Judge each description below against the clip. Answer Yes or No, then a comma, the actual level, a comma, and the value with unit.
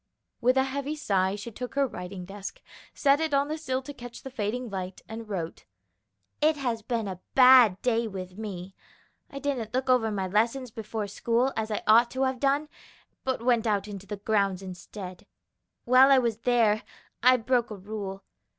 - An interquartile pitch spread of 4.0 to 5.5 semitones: Yes, average, 4.4 semitones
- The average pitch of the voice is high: Yes, high, 230 Hz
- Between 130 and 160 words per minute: No, average, 185 wpm